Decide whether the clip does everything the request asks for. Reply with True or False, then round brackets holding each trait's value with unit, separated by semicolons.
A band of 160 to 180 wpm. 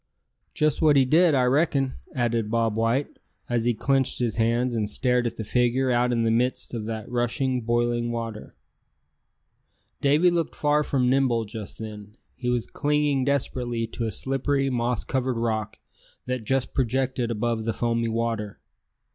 True (165 wpm)